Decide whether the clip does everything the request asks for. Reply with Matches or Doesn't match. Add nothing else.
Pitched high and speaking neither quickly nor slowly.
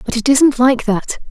Doesn't match